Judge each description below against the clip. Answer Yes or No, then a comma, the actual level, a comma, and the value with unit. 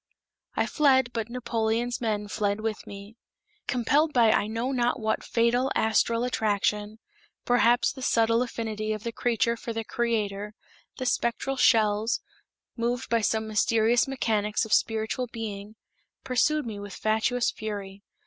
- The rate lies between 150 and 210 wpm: No, average, 140 wpm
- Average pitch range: No, narrow, 2.1 semitones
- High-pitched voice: Yes, high, 225 Hz